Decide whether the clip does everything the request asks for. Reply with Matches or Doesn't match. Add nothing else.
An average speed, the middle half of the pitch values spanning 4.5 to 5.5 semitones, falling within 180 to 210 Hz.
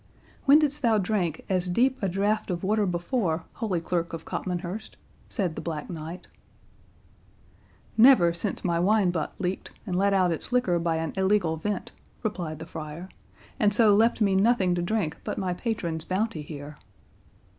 Doesn't match